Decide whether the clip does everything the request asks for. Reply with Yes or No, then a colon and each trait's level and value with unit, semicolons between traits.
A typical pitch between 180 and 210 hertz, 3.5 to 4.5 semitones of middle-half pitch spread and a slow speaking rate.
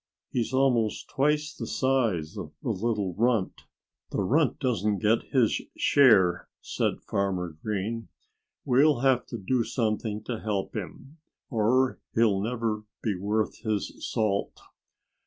No: low, 110 Hz; average, 3.8 semitones; slow, 130 wpm